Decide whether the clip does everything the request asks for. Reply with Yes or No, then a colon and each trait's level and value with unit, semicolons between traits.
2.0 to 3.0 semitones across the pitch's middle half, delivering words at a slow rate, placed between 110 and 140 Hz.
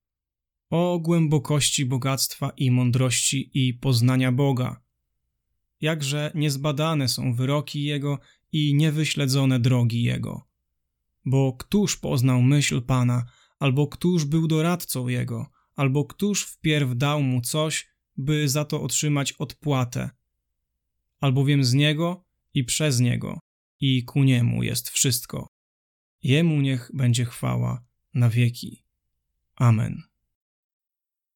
No: average, 3.6 semitones; slow, 105 wpm; low, 135 Hz